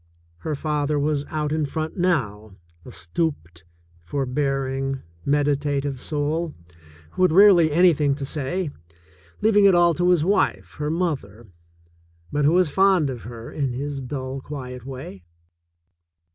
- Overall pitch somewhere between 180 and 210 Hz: No, medium, 145 Hz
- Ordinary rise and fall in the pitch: Yes, average, 3.6 semitones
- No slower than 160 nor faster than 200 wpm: No, average, 145 wpm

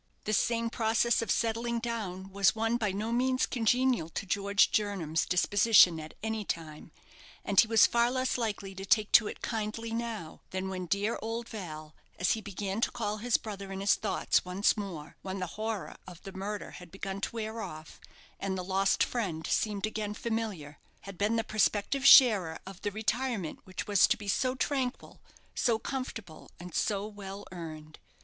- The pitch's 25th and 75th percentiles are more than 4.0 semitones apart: No, average, 3.3 semitones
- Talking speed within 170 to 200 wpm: Yes, average, 185 wpm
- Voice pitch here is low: No, high, 205 Hz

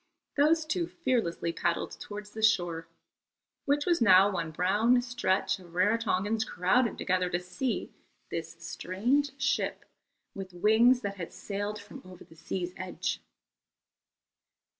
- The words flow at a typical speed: No, slow, 130 wpm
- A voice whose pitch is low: No, high, 205 Hz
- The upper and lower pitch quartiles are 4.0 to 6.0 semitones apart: Yes, average, 5.3 semitones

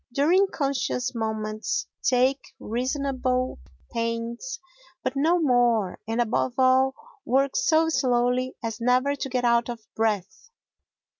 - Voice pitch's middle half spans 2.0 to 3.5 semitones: Yes, average, 2.8 semitones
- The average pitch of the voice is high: Yes, very high, 250 Hz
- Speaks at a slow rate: Yes, slow, 120 wpm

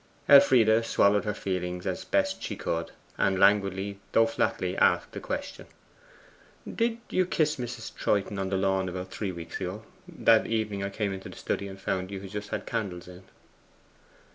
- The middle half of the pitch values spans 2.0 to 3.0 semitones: Yes, average, 2.7 semitones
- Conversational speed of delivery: Yes, average, 175 wpm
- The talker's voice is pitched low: Yes, low, 100 Hz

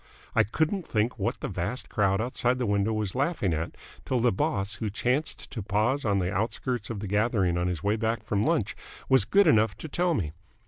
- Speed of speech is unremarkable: No, fast, 215 wpm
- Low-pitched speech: Yes, low, 110 Hz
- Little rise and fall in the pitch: No, average, 4.1 semitones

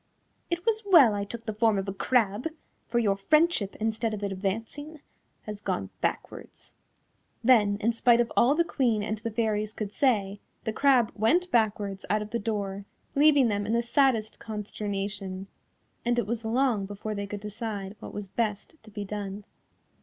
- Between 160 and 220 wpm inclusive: Yes, average, 175 wpm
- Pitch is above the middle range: Yes, high, 215 Hz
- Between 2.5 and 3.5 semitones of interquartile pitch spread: Yes, average, 2.8 semitones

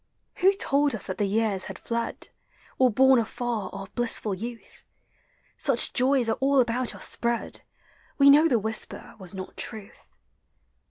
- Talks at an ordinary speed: Yes, average, 155 wpm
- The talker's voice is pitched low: No, high, 235 Hz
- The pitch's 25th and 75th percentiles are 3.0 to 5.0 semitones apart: Yes, average, 3.8 semitones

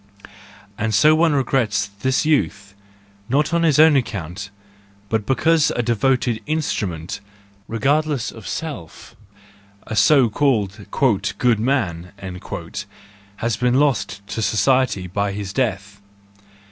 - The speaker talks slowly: Yes, slow, 110 wpm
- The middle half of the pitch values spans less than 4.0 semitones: No, wide, 5.4 semitones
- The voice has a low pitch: Yes, low, 115 Hz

